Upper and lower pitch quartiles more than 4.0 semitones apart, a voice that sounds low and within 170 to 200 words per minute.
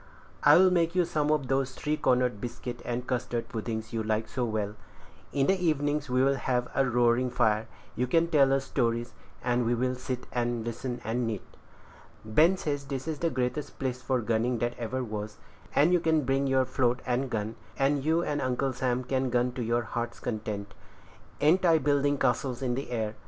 No: average, 2.8 semitones; low, 125 Hz; average, 195 wpm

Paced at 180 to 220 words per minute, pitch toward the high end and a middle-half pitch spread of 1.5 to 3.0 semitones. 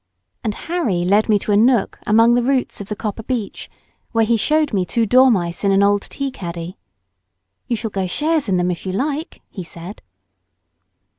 No: average, 195 wpm; high, 215 Hz; average, 4.7 semitones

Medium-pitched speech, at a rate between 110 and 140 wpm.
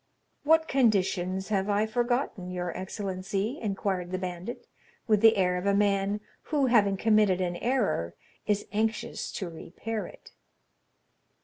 No: high, 200 Hz; slow, 135 wpm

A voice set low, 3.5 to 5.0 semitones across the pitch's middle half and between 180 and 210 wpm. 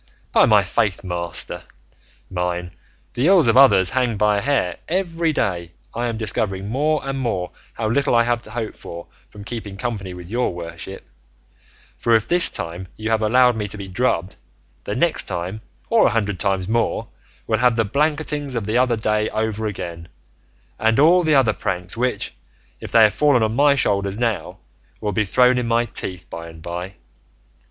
Yes: low, 110 Hz; average, 4.7 semitones; average, 185 wpm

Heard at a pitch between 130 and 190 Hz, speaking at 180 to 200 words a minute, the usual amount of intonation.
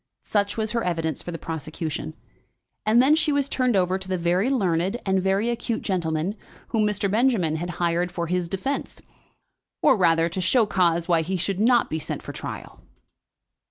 Yes: medium, 185 Hz; average, 185 wpm; average, 4.5 semitones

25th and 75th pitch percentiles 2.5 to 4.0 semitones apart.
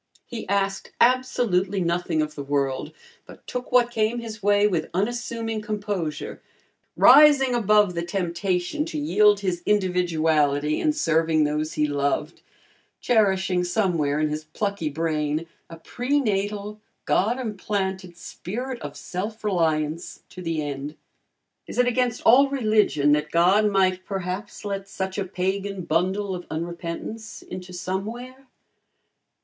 No: average, 4.6 semitones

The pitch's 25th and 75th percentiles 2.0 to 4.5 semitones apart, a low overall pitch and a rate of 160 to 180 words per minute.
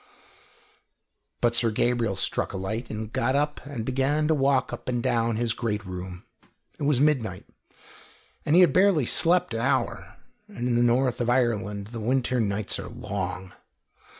Yes: average, 3.8 semitones; low, 120 Hz; average, 170 wpm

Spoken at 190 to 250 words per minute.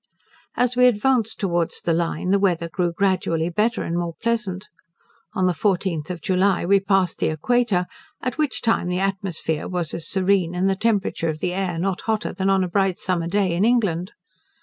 Yes: average, 195 wpm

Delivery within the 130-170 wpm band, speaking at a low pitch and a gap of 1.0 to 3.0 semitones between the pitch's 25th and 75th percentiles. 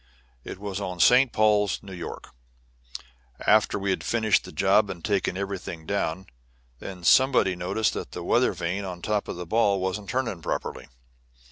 Yes: average, 165 wpm; low, 100 Hz; narrow, 2.6 semitones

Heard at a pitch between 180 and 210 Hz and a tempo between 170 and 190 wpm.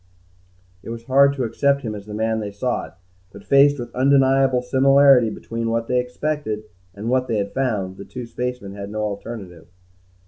No: low, 120 Hz; average, 180 wpm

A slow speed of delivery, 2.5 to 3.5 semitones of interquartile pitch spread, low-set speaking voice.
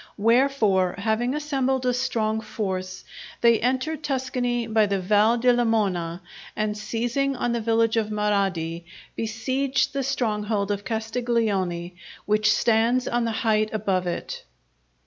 No: slow, 130 wpm; average, 2.9 semitones; high, 225 Hz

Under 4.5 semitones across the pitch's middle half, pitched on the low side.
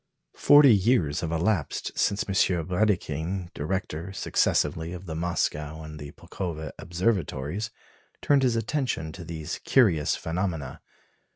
Yes: average, 4.1 semitones; very low, 85 Hz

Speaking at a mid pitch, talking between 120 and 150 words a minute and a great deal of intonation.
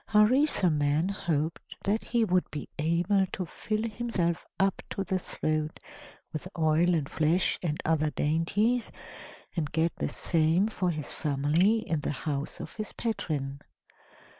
No: medium, 170 Hz; average, 140 wpm; average, 4.5 semitones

